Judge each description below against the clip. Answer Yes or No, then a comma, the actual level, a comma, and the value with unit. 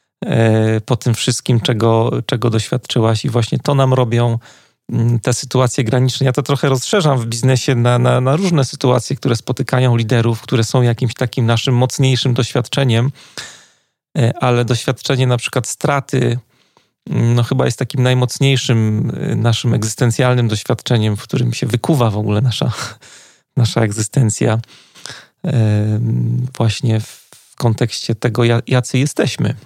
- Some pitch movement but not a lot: No, narrow, 2.1 semitones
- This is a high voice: No, low, 125 Hz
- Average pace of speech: Yes, average, 125 wpm